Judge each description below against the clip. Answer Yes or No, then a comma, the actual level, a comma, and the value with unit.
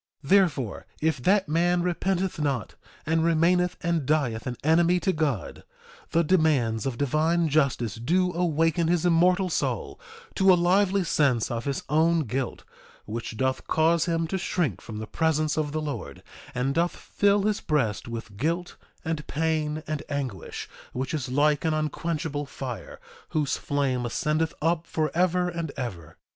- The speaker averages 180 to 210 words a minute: No, average, 155 wpm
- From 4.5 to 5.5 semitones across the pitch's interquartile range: No, average, 4.0 semitones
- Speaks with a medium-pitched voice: Yes, medium, 155 Hz